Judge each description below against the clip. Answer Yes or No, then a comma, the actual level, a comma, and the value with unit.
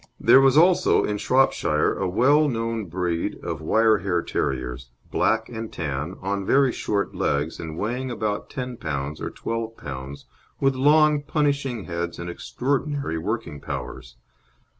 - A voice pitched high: No, low, 105 Hz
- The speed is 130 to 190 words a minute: Yes, average, 145 wpm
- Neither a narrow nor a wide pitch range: No, wide, 8.3 semitones